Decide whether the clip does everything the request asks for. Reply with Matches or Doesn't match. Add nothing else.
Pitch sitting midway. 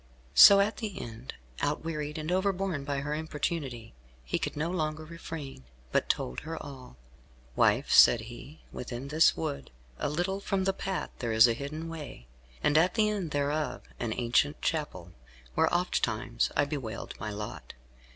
Matches